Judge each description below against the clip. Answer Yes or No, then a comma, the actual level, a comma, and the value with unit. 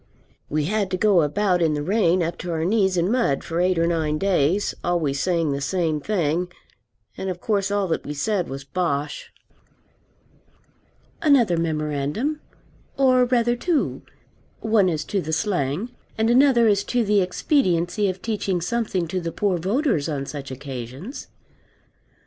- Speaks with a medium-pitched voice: Yes, medium, 180 Hz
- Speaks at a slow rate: No, average, 160 wpm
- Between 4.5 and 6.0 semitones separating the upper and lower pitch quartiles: Yes, average, 5.3 semitones